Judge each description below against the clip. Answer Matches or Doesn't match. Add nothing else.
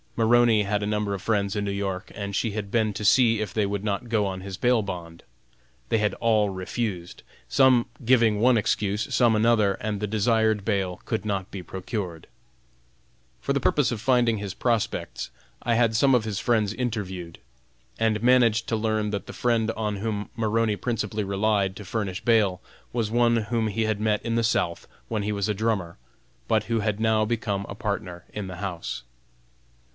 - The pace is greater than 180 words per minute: Matches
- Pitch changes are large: Doesn't match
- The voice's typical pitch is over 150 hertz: Doesn't match